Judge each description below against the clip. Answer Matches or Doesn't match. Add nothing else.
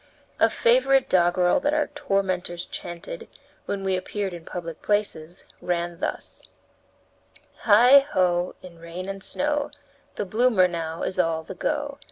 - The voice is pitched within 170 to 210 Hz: Matches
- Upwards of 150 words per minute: Doesn't match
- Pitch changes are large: Matches